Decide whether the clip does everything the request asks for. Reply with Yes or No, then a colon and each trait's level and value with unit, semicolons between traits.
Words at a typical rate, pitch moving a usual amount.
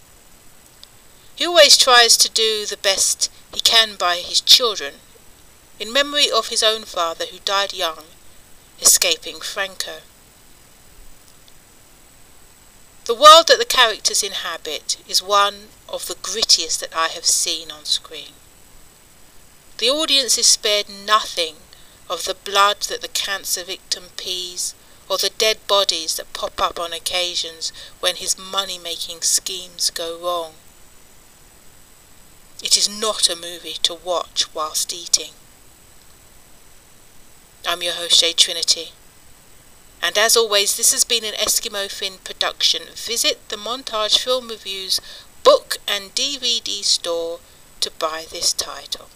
No: slow, 130 wpm; average, 5.0 semitones